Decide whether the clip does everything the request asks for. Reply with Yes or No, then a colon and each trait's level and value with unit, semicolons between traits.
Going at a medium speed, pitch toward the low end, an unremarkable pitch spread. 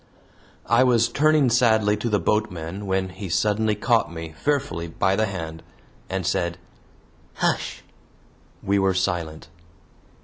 No: slow, 130 wpm; low, 100 Hz; average, 4.2 semitones